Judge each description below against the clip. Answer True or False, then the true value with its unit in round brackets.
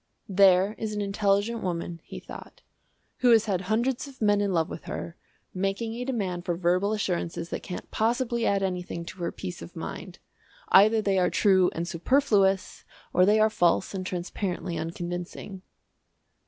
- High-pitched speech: True (195 Hz)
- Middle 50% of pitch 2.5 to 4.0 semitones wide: True (3.5 semitones)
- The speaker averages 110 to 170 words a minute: True (165 wpm)